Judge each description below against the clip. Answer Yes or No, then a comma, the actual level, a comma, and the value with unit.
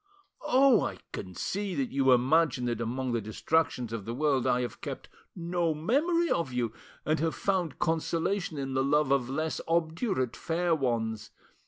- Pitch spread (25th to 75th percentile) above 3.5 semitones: Yes, average, 5.2 semitones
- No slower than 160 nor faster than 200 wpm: Yes, average, 170 wpm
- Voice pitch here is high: No, medium, 150 Hz